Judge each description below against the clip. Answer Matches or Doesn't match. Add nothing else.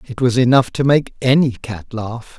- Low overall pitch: Matches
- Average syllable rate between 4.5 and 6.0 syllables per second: Matches